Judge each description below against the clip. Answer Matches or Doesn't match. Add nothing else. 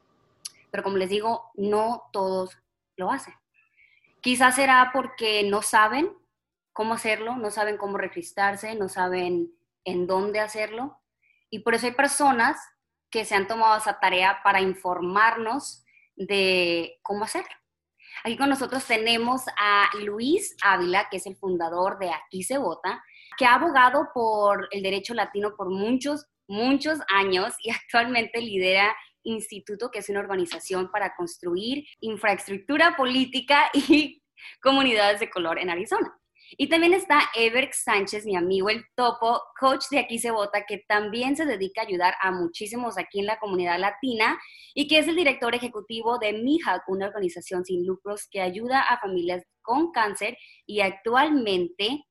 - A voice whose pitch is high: Matches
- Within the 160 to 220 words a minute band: Doesn't match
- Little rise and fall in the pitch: Doesn't match